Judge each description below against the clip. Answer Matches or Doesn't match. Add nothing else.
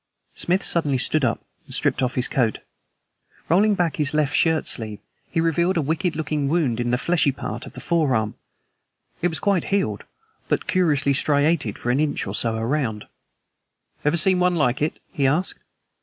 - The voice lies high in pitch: Doesn't match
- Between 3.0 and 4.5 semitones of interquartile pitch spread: Doesn't match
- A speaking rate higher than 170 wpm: Matches